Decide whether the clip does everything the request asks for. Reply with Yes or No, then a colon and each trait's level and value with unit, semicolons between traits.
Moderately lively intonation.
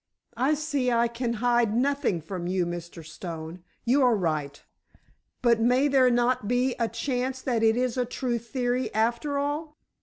Yes: average, 3.5 semitones